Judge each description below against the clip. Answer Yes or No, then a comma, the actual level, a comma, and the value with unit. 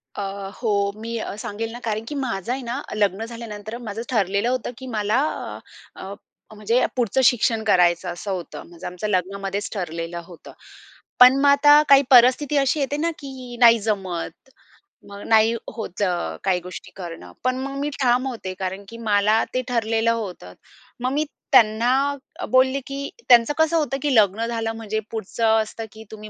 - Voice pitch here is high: Yes, high, 225 Hz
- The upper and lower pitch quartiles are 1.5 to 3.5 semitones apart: No, average, 4.0 semitones